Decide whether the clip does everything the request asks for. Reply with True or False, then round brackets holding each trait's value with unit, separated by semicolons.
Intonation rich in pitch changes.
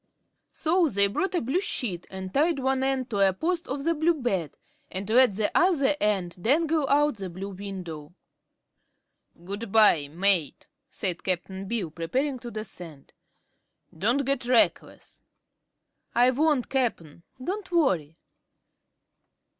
True (6.9 semitones)